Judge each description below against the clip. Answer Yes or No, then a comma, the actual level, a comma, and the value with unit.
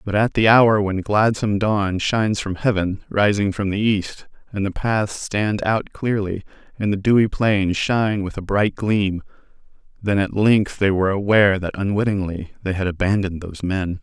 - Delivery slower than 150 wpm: No, average, 180 wpm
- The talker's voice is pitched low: Yes, low, 100 Hz